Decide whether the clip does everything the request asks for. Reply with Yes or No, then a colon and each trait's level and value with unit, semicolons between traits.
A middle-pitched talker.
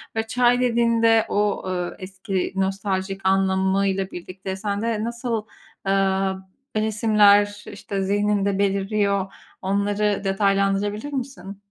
No: high, 200 Hz